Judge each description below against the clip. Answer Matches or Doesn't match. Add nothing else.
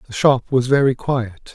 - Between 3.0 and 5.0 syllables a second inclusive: Matches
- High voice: Doesn't match